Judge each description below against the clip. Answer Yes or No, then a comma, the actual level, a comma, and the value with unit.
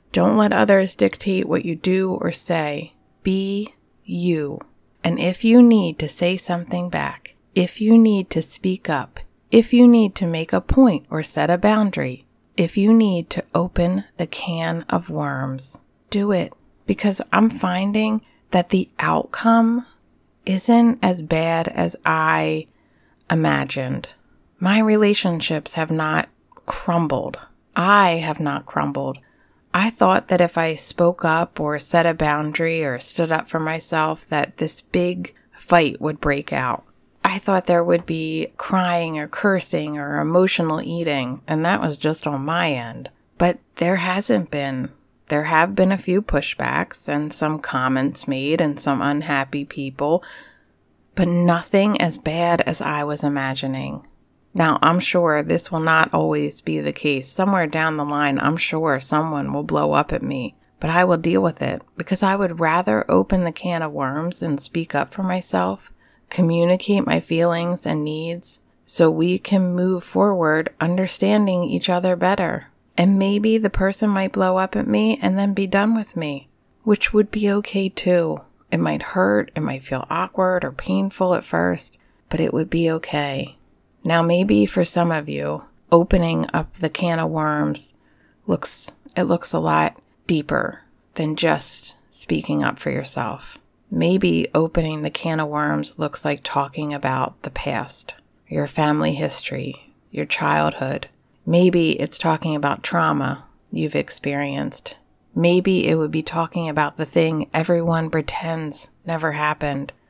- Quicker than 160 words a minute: No, average, 155 wpm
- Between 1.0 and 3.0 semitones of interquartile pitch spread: No, average, 3.9 semitones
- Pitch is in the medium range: Yes, medium, 165 Hz